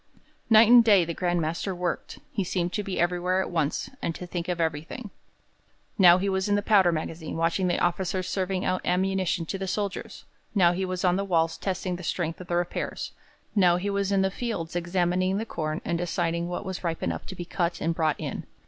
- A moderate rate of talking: No, fast, 220 wpm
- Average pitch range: No, narrow, 2.0 semitones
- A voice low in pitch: No, medium, 180 Hz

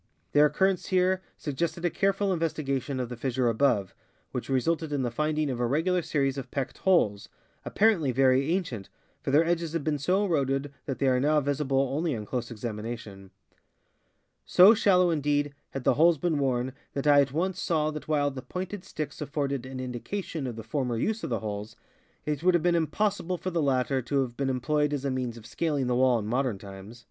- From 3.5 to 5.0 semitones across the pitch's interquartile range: Yes, average, 4.6 semitones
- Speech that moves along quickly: Yes, fast, 210 wpm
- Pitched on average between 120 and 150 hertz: Yes, medium, 140 Hz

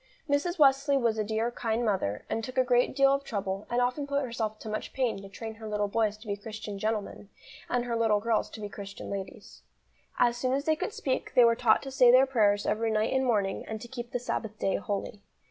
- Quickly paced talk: Yes, fast, 240 wpm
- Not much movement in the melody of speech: No, average, 3.3 semitones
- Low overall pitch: No, high, 225 Hz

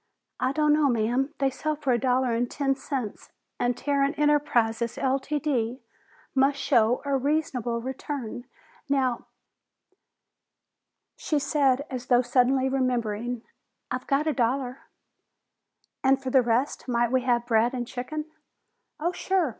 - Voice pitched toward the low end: No, very high, 260 Hz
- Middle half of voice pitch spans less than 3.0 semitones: Yes, narrow, 2.5 semitones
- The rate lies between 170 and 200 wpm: No, average, 140 wpm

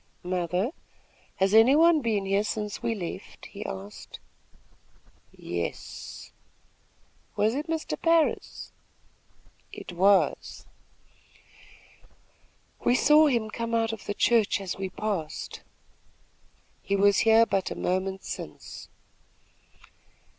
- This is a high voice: Yes, high, 210 Hz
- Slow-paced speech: Yes, slow, 105 wpm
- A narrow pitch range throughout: No, average, 3.4 semitones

